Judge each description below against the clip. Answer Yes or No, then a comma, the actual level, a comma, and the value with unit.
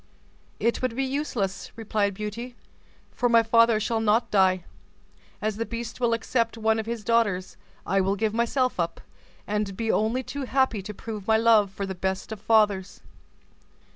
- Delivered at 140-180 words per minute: Yes, average, 170 wpm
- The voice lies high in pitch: Yes, high, 220 Hz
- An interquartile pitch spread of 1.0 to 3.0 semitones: Yes, narrow, 2.5 semitones